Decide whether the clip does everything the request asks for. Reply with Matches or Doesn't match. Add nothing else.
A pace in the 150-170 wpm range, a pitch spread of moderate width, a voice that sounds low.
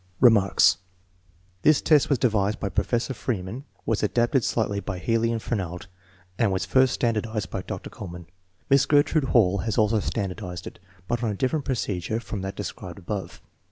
Matches